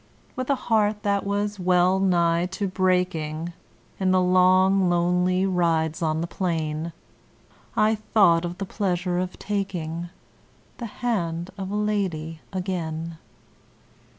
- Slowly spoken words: Yes, slow, 125 wpm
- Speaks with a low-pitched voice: No, medium, 180 Hz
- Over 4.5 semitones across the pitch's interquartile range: No, average, 2.7 semitones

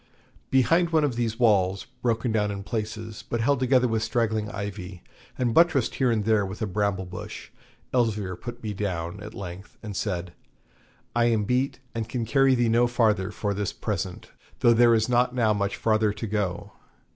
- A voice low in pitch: Yes, low, 110 Hz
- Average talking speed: Yes, average, 185 wpm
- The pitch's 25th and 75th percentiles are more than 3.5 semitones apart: No, average, 3.0 semitones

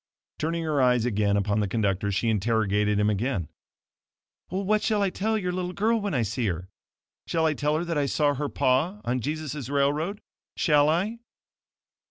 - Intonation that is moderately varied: No, wide, 8.1 semitones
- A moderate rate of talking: Yes, average, 180 wpm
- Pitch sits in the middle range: Yes, medium, 145 Hz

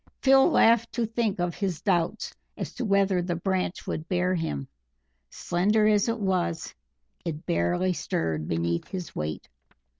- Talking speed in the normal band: Yes, average, 150 wpm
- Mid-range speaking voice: Yes, medium, 180 Hz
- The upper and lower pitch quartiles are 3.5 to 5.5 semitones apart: Yes, average, 4.2 semitones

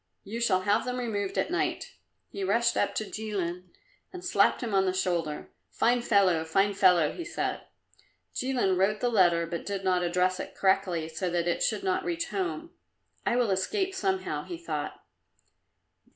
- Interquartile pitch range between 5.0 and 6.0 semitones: Yes, wide, 5.4 semitones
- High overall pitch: Yes, high, 200 Hz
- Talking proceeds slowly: No, average, 175 wpm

